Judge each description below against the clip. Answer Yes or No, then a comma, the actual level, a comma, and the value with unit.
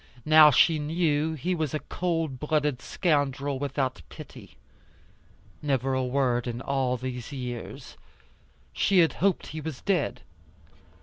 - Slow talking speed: Yes, slow, 130 wpm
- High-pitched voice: No, medium, 145 Hz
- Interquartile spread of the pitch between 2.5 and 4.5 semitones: Yes, average, 3.5 semitones